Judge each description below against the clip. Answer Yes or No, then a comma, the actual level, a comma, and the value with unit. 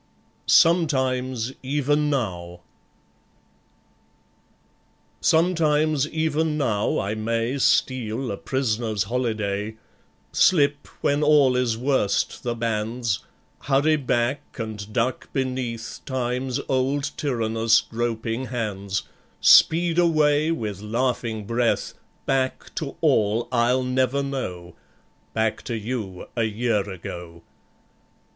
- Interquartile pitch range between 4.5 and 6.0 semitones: No, average, 4.1 semitones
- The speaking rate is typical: No, slow, 95 wpm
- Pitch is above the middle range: No, low, 125 Hz